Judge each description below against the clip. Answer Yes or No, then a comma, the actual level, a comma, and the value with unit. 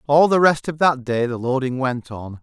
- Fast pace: Yes, fast, 245 wpm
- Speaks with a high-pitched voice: No, low, 135 Hz